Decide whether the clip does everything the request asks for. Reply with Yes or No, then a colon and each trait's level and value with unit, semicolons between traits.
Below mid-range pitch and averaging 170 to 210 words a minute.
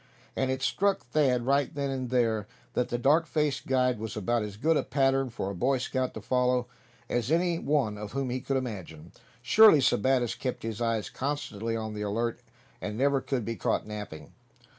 Yes: low, 125 Hz; average, 190 wpm